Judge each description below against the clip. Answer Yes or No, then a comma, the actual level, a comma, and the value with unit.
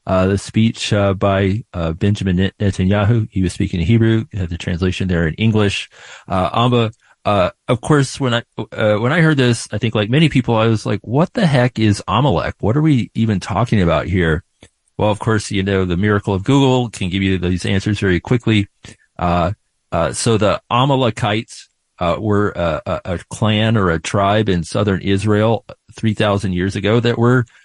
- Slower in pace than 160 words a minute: No, average, 200 wpm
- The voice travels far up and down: No, average, 3.3 semitones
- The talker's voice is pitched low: Yes, low, 105 Hz